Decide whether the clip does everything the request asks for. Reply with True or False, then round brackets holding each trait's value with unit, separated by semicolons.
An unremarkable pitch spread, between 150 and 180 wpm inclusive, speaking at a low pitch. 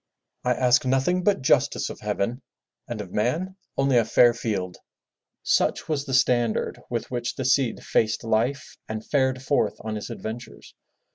True (3.1 semitones; 160 wpm; 125 Hz)